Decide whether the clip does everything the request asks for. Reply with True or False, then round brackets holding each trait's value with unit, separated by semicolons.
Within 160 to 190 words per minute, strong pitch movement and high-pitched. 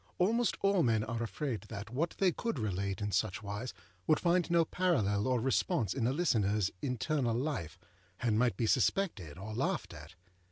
False (175 wpm; 7.4 semitones; 115 Hz)